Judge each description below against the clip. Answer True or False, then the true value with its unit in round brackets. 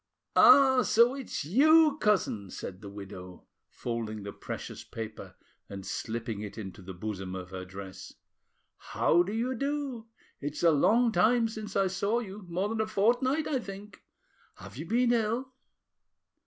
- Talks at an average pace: True (155 wpm)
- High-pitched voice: True (195 Hz)